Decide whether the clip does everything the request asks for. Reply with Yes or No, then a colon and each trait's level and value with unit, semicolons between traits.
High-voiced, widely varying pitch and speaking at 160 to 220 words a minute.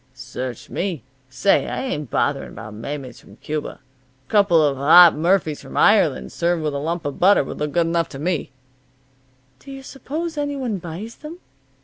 No: medium, 165 Hz; wide, 6.1 semitones; average, 180 wpm